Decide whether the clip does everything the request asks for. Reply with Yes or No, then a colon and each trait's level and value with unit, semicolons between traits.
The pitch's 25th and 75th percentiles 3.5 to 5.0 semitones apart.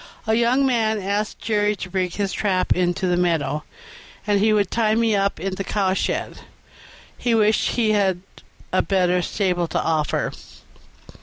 No: average, 3.0 semitones